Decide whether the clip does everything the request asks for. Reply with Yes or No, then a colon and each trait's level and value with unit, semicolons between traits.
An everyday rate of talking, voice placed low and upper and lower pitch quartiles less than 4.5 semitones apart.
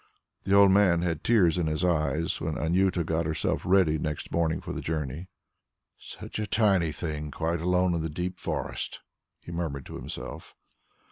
Yes: average, 175 wpm; very low, 85 Hz; average, 2.7 semitones